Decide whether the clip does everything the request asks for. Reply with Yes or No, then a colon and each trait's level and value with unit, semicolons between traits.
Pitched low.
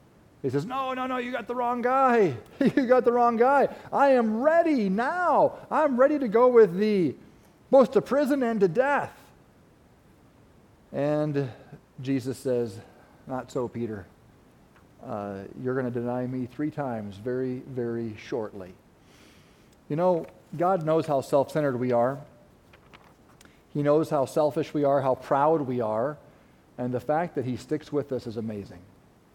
No: medium, 145 Hz